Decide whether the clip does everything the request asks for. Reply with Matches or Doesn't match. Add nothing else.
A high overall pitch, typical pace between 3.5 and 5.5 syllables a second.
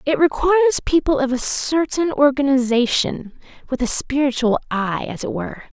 Matches